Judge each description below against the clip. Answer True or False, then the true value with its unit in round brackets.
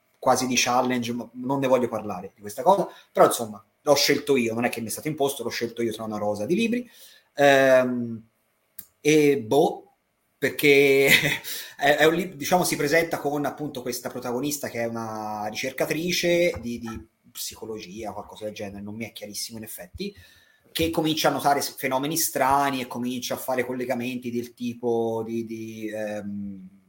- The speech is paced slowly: False (170 wpm)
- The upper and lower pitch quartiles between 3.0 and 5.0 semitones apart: True (4.3 semitones)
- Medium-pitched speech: False (125 Hz)